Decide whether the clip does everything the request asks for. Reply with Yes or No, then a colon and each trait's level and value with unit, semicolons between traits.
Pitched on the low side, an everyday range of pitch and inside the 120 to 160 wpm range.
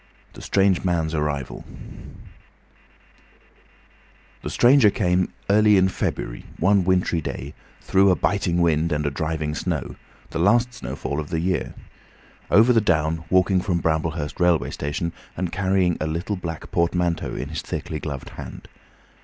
Yes: very low, 85 Hz; average, 3.3 semitones; average, 145 wpm